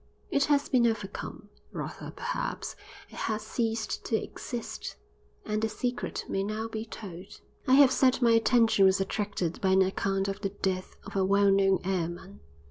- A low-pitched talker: No, high, 210 Hz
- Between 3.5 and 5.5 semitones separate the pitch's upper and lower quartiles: No, average, 3.0 semitones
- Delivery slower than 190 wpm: Yes, average, 170 wpm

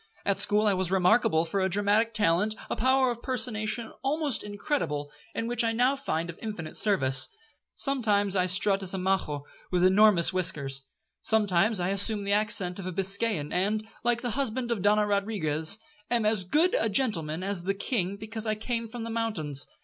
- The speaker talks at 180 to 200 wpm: Yes, average, 185 wpm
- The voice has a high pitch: Yes, high, 205 Hz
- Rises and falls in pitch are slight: No, average, 3.7 semitones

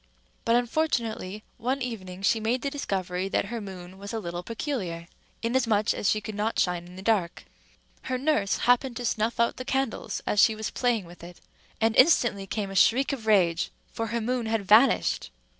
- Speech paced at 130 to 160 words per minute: No, average, 190 wpm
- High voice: Yes, high, 220 Hz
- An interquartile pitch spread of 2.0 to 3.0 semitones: No, average, 3.9 semitones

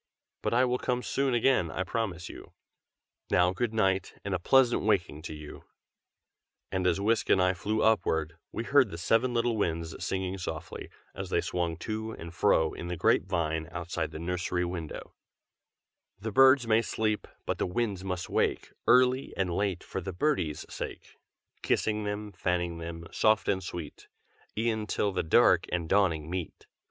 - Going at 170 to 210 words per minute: Yes, average, 175 wpm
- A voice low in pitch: Yes, very low, 95 Hz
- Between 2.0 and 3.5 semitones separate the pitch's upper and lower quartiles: No, average, 4.5 semitones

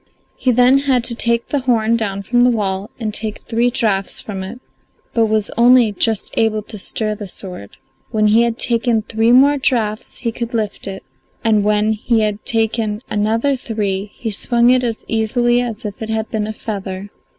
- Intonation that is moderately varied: No, narrow, 2.2 semitones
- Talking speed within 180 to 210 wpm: Yes, average, 195 wpm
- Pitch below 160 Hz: No, high, 220 Hz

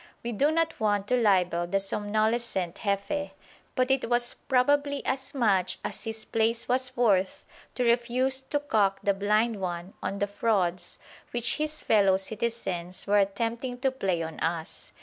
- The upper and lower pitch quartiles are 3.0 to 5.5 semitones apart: Yes, average, 4.4 semitones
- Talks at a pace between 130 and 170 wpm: Yes, average, 160 wpm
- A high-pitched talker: Yes, high, 220 Hz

